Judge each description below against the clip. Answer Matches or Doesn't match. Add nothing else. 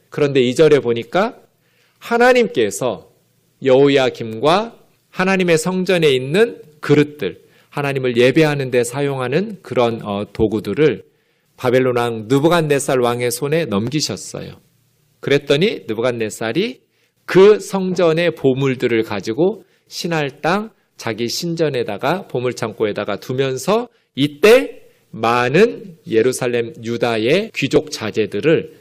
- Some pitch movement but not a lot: Doesn't match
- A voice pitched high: Doesn't match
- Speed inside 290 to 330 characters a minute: Doesn't match